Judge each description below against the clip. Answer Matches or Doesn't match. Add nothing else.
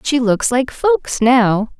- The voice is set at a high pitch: Matches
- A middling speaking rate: Matches